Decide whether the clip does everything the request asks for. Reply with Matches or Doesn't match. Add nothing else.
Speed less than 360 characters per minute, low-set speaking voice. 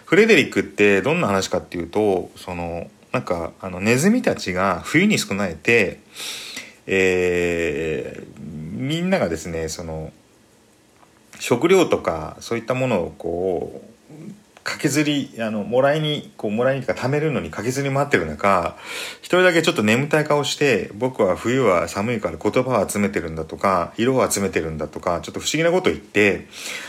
Matches